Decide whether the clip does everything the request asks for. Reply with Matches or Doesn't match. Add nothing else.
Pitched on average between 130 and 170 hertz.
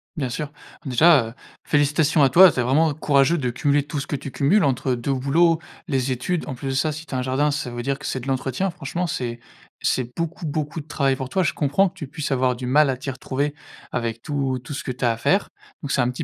Matches